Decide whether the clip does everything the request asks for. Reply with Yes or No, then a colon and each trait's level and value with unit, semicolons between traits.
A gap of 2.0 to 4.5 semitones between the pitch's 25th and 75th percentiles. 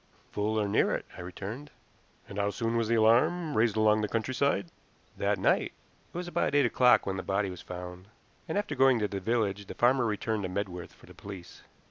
Yes: average, 3.8 semitones